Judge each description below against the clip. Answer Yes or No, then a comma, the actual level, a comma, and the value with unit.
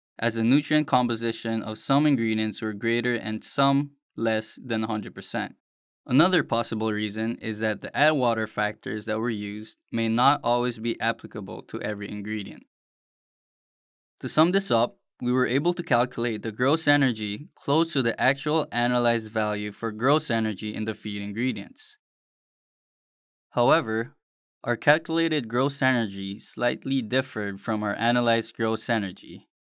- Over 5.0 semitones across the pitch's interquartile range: No, average, 3.6 semitones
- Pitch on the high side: No, low, 115 Hz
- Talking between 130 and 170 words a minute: Yes, average, 145 wpm